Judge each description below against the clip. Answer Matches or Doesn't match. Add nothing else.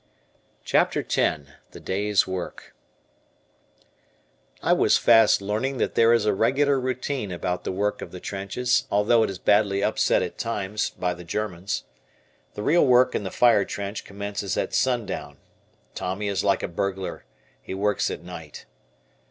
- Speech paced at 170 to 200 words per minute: Doesn't match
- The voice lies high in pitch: Doesn't match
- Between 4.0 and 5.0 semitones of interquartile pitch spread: Doesn't match